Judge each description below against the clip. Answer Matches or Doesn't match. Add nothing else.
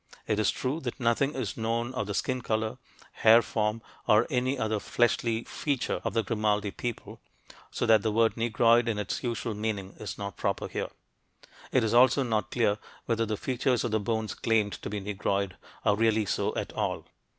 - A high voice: Doesn't match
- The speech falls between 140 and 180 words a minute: Doesn't match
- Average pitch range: Doesn't match